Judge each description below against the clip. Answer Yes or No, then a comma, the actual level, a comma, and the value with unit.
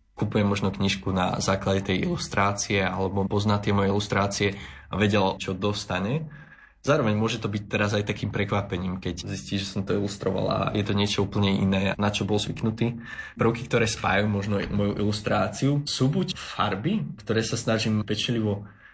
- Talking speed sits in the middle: No, fast, 170 wpm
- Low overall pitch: Yes, low, 105 Hz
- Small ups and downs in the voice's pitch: Yes, narrow, 2.3 semitones